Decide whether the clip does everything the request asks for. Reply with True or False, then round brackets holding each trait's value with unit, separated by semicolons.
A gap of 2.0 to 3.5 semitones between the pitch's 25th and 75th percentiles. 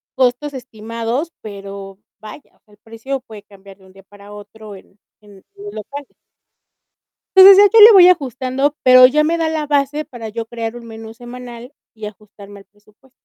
False (4.9 semitones)